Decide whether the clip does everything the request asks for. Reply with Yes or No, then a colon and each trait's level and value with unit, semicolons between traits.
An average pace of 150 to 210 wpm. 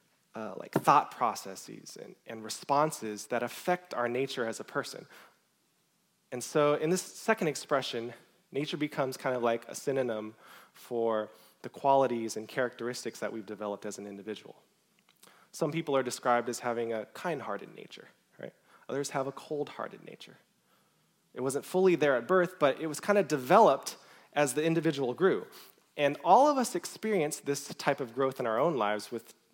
Yes: average, 170 wpm